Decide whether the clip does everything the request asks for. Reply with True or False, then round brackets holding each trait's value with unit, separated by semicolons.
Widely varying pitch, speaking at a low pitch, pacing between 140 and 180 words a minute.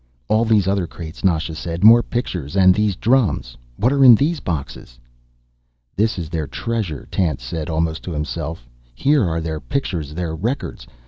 True (5.7 semitones; 85 Hz; 170 wpm)